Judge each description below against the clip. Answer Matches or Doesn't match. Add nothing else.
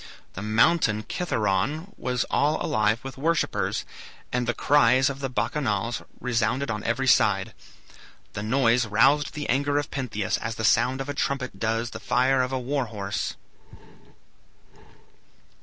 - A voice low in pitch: Matches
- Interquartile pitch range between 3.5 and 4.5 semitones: Matches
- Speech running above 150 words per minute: Doesn't match